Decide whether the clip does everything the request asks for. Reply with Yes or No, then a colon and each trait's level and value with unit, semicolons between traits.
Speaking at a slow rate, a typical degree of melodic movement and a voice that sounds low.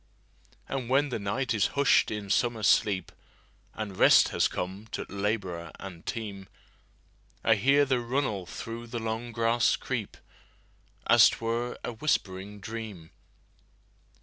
Yes: slow, 120 wpm; average, 3.3 semitones; low, 110 Hz